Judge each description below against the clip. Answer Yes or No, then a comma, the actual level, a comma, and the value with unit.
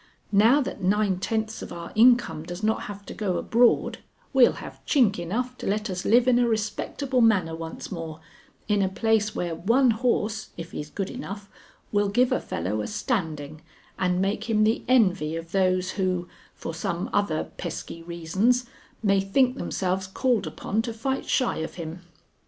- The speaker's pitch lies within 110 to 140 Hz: No, high, 200 Hz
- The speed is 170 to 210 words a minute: Yes, average, 175 wpm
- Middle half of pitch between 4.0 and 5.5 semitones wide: Yes, average, 4.5 semitones